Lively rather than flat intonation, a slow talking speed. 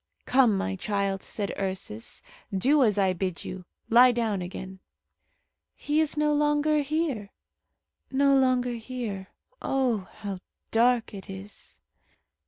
Yes: wide, 5.7 semitones; slow, 125 wpm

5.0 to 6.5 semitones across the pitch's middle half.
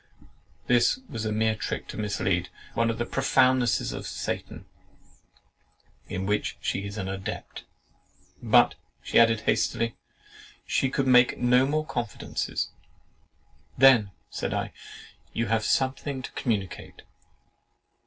No: average, 3.5 semitones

